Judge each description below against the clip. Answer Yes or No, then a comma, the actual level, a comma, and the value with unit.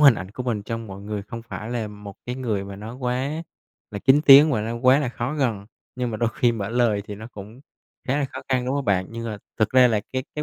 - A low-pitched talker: Yes, low, 115 Hz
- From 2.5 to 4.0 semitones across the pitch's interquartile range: Yes, average, 3.7 semitones